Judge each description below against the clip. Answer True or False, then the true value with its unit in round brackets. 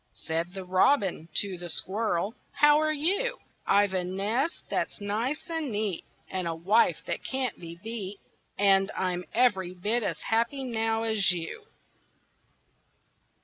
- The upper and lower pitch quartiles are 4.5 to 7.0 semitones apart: True (4.8 semitones)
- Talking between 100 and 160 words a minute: True (145 wpm)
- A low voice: False (205 Hz)